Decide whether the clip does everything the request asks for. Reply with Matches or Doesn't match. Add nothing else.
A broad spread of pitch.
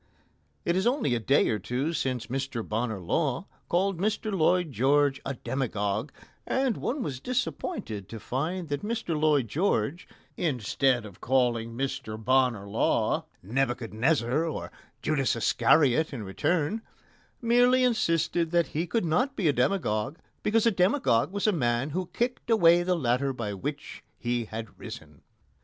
Matches